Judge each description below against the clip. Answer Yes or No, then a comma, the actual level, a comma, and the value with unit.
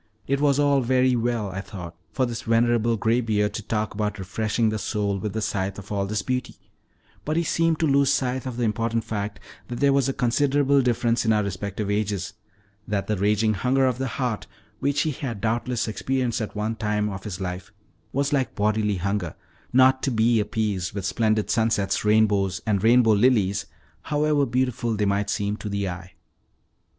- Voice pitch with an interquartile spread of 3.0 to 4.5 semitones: Yes, average, 3.8 semitones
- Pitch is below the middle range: Yes, low, 110 Hz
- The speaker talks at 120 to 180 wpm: No, average, 190 wpm